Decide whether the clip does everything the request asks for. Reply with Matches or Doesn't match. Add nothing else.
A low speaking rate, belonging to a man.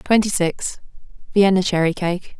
Doesn't match